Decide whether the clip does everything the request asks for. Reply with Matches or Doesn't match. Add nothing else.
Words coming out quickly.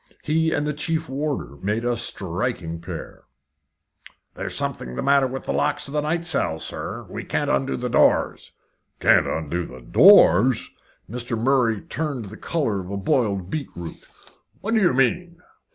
Doesn't match